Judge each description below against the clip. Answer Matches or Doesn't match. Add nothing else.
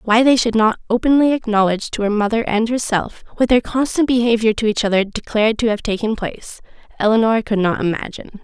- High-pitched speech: Matches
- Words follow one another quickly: Doesn't match